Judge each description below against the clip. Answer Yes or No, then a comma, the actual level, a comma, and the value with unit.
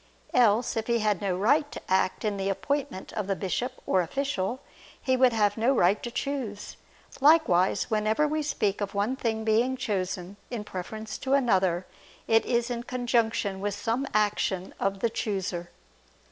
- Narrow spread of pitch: No, average, 4.1 semitones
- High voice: Yes, high, 215 Hz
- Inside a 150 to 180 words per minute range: Yes, average, 170 wpm